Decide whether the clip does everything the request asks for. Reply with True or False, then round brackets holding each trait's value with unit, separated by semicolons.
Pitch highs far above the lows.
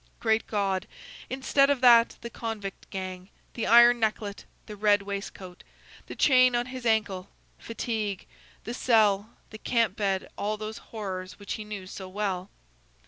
False (3.0 semitones)